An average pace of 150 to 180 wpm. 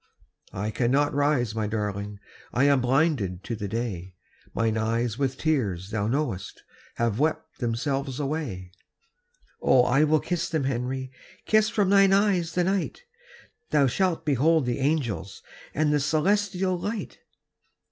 No: average, 140 wpm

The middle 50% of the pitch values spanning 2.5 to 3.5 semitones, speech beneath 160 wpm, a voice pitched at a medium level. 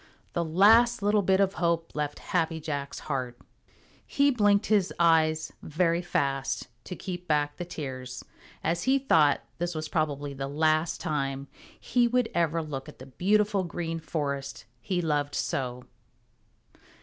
No: average, 4.3 semitones; average, 150 wpm; medium, 160 Hz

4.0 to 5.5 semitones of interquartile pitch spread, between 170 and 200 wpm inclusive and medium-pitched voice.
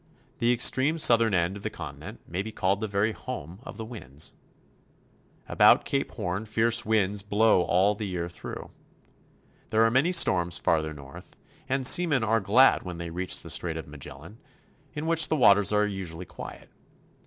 No: average, 4.4 semitones; average, 175 wpm; low, 105 Hz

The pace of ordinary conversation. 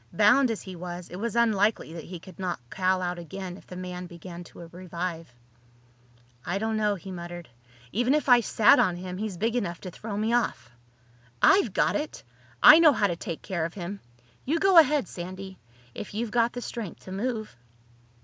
Yes: average, 195 wpm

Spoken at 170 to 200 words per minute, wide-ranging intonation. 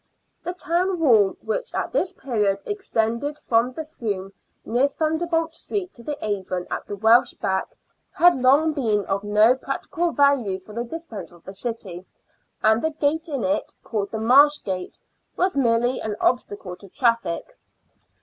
No: average, 160 wpm; wide, 7.3 semitones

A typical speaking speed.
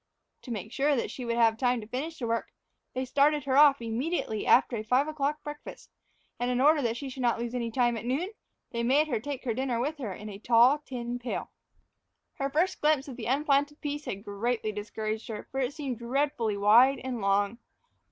No: fast, 220 wpm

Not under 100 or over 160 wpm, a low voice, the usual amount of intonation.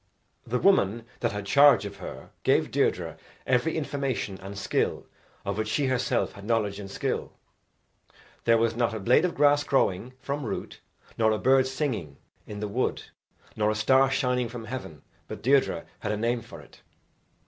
No: average, 175 wpm; low, 115 Hz; average, 4.0 semitones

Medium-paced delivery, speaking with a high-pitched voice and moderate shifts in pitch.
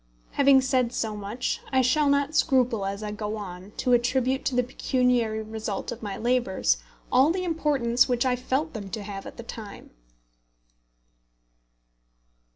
Yes: average, 160 wpm; high, 245 Hz; average, 3.6 semitones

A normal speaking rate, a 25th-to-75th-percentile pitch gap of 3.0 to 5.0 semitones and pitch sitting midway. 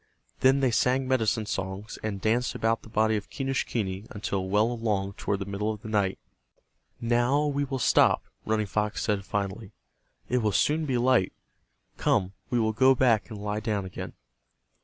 No: average, 175 wpm; average, 3.5 semitones; low, 110 Hz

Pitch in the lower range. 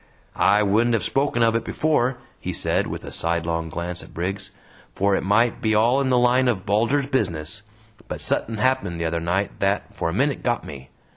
Yes: low, 105 Hz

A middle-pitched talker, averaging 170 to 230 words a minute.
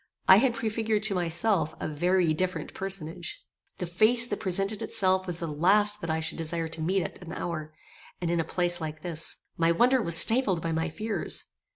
Yes: medium, 180 Hz; average, 200 wpm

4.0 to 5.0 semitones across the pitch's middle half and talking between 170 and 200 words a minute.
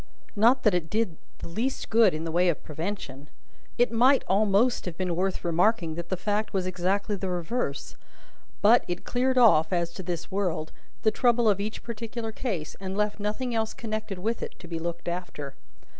Yes: average, 4.5 semitones; average, 190 wpm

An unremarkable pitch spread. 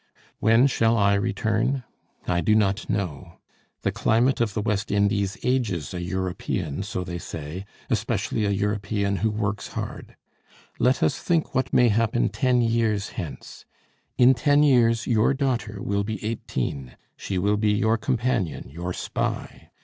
Yes: average, 3.0 semitones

